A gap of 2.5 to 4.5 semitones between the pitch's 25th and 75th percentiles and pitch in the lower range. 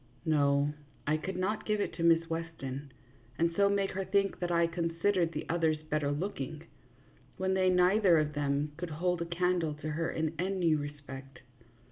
No: average, 3.3 semitones; medium, 165 Hz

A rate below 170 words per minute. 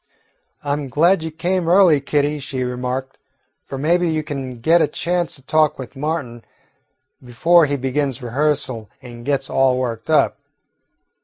Yes: average, 155 wpm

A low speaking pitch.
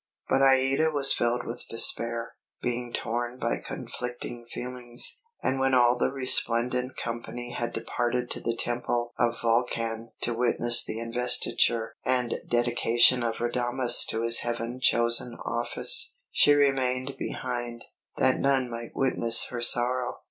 Yes: low, 120 Hz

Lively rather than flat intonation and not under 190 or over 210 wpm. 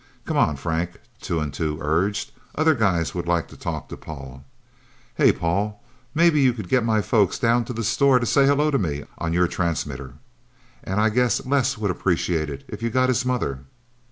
Yes: wide, 7.2 semitones; average, 200 wpm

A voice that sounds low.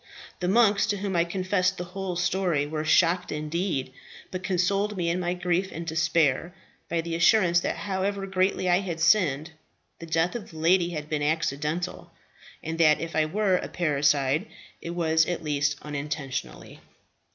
No: medium, 170 Hz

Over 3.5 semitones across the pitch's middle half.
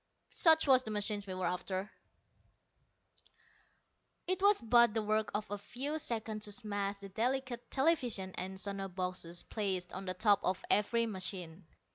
Yes: average, 3.9 semitones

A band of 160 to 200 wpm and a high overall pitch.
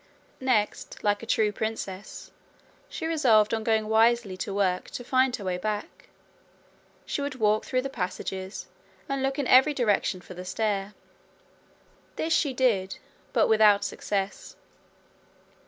No: average, 140 wpm; high, 215 Hz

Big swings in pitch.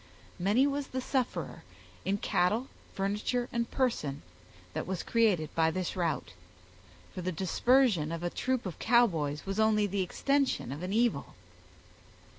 Yes: wide, 5.7 semitones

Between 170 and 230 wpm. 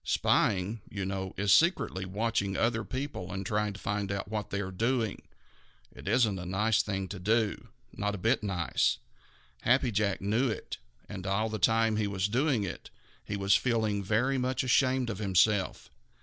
Yes: average, 175 wpm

